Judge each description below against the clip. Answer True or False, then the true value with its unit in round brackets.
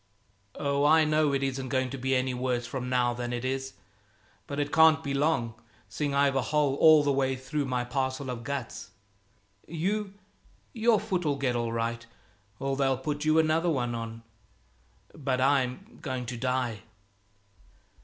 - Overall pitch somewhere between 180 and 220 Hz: False (135 Hz)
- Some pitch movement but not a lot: True (3.2 semitones)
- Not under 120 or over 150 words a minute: False (165 wpm)